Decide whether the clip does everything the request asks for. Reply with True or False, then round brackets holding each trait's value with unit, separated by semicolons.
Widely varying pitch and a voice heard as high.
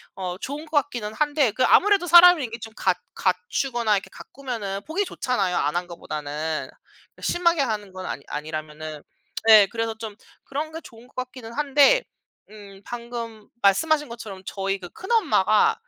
True (7.0 semitones; 225 Hz)